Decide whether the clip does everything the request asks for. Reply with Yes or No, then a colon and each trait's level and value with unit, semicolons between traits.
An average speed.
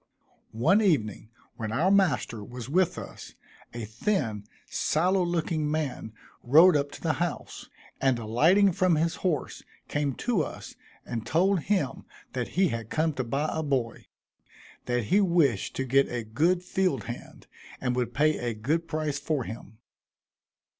Yes: average, 155 wpm